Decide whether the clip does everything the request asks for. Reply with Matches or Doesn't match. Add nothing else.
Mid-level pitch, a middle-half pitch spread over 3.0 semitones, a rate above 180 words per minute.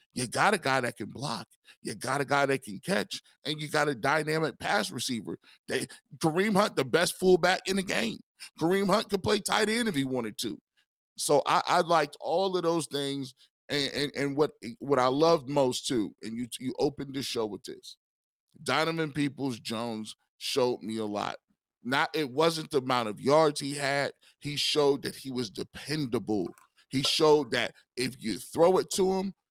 Matches